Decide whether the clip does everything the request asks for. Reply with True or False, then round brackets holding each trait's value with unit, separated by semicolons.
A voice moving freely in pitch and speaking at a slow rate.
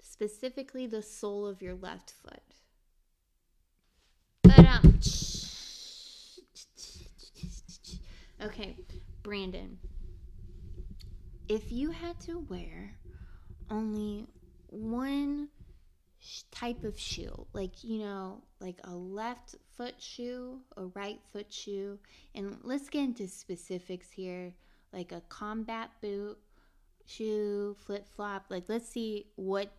False (3.8 semitones; 105 wpm)